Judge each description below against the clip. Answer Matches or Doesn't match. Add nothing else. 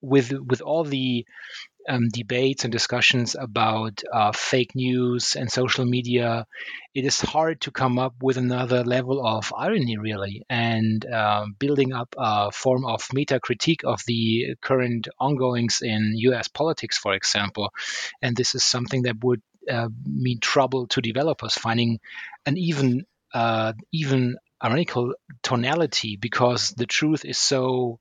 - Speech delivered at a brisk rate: Doesn't match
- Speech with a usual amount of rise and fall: Doesn't match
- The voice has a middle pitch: Doesn't match